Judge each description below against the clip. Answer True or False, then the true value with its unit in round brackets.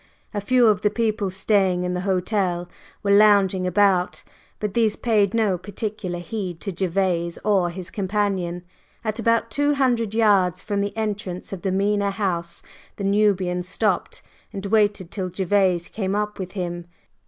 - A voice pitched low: False (195 Hz)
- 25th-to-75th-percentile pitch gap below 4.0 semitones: True (2.5 semitones)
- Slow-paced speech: False (160 wpm)